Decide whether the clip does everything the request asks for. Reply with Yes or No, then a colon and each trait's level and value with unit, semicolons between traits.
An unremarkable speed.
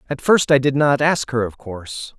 No: fast, 245 wpm